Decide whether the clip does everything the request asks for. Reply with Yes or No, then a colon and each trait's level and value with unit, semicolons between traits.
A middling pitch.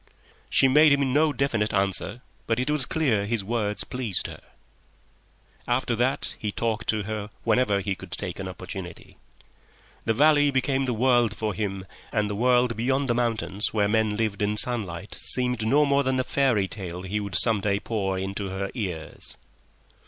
No: low, 110 Hz